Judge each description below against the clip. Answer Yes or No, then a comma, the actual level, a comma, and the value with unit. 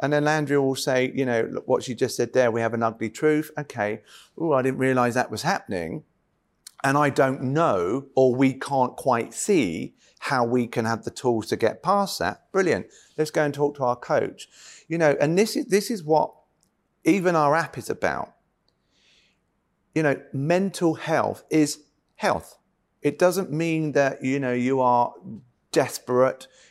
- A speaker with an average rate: Yes, average, 180 wpm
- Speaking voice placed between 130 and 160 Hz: Yes, medium, 140 Hz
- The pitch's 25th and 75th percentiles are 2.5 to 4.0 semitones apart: Yes, average, 3.6 semitones